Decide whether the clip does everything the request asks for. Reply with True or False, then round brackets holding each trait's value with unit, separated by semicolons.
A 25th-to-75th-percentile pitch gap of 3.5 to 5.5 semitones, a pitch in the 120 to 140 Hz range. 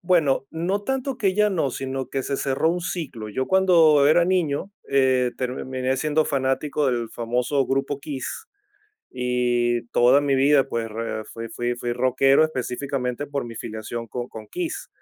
True (4.0 semitones; 135 Hz)